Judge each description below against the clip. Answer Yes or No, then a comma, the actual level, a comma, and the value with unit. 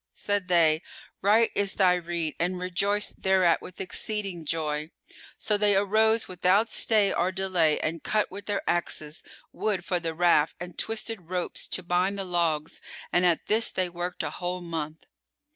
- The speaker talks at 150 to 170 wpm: Yes, average, 165 wpm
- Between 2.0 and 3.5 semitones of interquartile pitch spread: Yes, average, 2.9 semitones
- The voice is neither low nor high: Yes, medium, 180 Hz